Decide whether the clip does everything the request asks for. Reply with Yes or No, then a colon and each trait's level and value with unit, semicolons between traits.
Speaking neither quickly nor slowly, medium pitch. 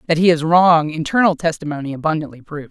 Yes: average, 180 wpm; medium, 160 Hz